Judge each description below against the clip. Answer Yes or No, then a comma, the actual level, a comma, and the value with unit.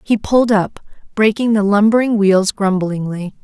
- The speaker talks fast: No, average, 140 wpm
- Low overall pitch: No, high, 205 Hz